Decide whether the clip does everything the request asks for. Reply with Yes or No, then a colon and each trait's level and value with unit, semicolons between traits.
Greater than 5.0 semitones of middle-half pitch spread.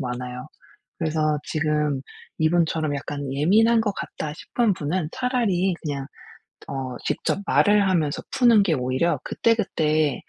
Yes: wide, 5.6 semitones